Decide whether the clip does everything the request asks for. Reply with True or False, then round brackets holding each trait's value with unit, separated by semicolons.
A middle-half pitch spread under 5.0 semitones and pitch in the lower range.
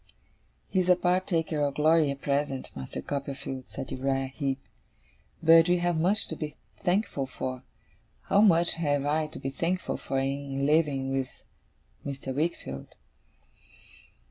False (3.7 semitones; 145 Hz)